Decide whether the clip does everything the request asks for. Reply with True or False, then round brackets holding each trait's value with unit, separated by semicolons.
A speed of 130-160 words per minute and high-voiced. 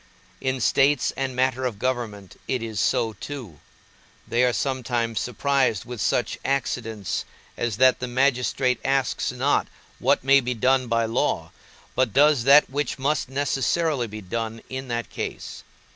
False (150 wpm; 125 Hz)